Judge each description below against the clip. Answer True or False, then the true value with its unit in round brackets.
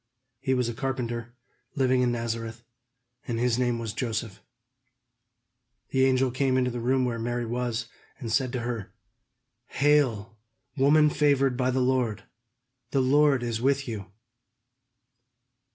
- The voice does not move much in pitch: True (2.2 semitones)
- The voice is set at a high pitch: False (125 Hz)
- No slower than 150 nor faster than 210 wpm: False (135 wpm)